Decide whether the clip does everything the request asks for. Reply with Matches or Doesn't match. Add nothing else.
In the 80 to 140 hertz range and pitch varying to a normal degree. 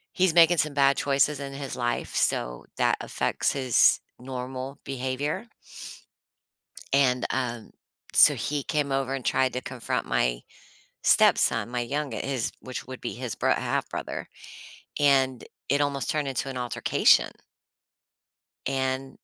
Doesn't match